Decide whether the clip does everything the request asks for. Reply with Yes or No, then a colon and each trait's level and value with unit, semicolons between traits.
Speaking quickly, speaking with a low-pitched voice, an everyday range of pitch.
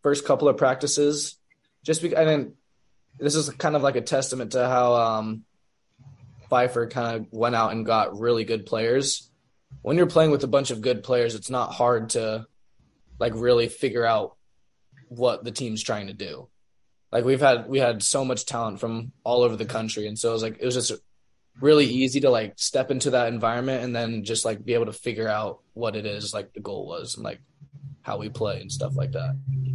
Yes: fast, 215 wpm; low, 120 Hz; average, 3.1 semitones